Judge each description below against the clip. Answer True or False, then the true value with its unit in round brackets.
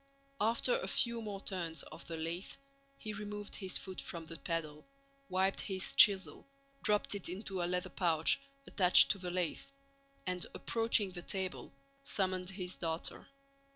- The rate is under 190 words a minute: True (155 wpm)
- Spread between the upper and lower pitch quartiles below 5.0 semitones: True (2.8 semitones)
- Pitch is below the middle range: False (185 Hz)